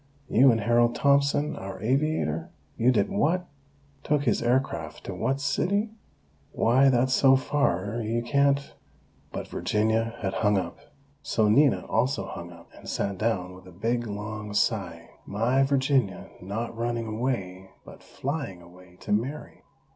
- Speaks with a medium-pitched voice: No, low, 115 Hz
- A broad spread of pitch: No, average, 5.0 semitones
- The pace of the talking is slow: No, average, 150 wpm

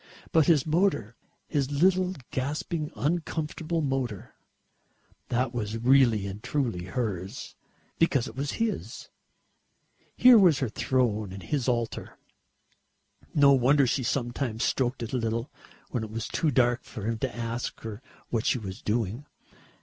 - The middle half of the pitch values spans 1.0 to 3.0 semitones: No, average, 4.4 semitones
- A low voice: Yes, low, 125 Hz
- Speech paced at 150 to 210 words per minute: No, average, 140 wpm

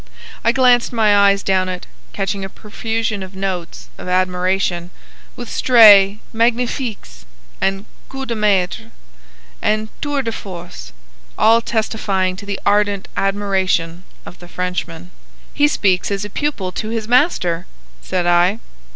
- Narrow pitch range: No, average, 3.5 semitones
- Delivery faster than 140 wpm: No, slow, 135 wpm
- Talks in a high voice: Yes, high, 200 Hz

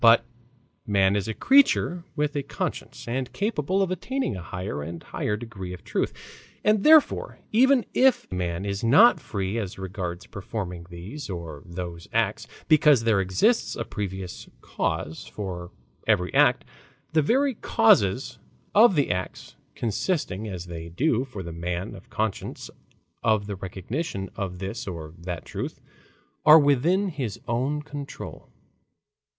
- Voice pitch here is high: No, low, 105 Hz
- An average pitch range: No, wide, 8.4 semitones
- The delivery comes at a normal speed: Yes, average, 145 wpm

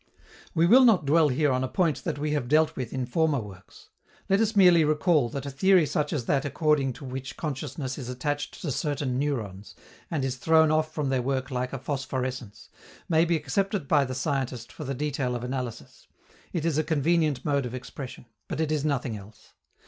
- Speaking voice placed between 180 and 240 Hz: No, medium, 140 Hz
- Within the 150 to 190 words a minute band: No, fast, 205 wpm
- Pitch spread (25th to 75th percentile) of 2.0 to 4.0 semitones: Yes, average, 3.4 semitones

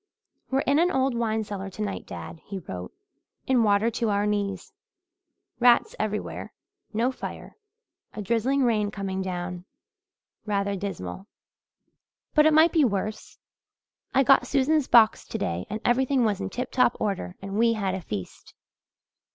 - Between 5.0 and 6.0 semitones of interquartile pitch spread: No, average, 4.5 semitones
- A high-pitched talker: Yes, high, 215 Hz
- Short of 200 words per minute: Yes, average, 150 wpm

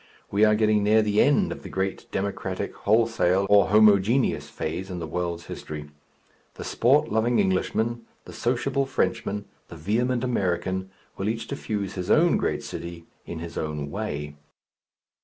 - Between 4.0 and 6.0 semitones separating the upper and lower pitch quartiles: Yes, average, 4.3 semitones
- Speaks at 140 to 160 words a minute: Yes, average, 155 wpm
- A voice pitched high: No, low, 105 Hz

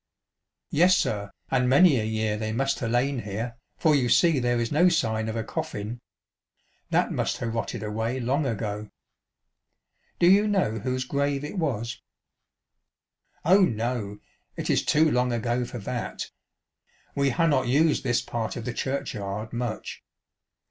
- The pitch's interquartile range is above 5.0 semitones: No, average, 4.1 semitones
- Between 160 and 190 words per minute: Yes, average, 170 wpm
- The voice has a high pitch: No, low, 120 Hz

